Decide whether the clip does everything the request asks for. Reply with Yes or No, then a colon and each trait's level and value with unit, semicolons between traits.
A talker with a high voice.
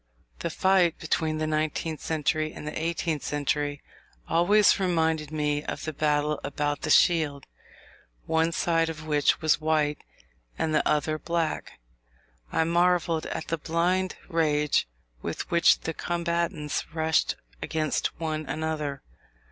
No: medium, 160 Hz